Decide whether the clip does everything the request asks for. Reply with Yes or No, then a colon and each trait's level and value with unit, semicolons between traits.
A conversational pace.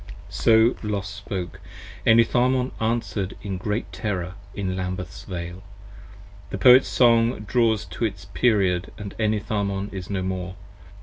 No: slow, 125 wpm